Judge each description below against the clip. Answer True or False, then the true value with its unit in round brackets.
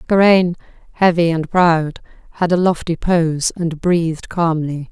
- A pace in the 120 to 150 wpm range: True (135 wpm)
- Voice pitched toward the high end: False (170 Hz)